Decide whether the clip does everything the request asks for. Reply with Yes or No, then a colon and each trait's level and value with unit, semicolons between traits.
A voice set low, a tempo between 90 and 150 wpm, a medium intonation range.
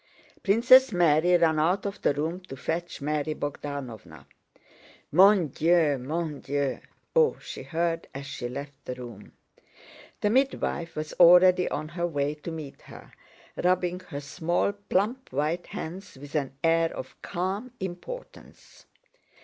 No: medium, 165 Hz; average, 140 wpm; average, 4.0 semitones